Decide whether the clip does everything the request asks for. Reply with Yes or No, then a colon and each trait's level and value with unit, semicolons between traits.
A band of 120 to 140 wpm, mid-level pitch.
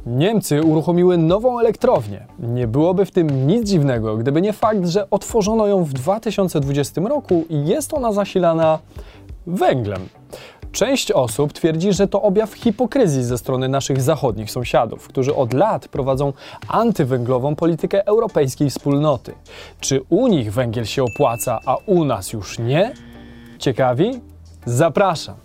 Yes: average, 135 wpm; medium, 155 Hz